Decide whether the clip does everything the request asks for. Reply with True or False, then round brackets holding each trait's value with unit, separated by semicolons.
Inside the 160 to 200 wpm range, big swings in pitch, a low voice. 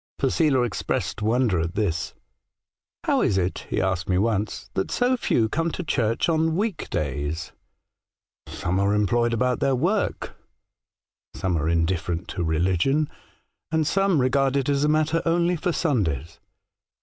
True (170 wpm; 9.0 semitones; 115 Hz)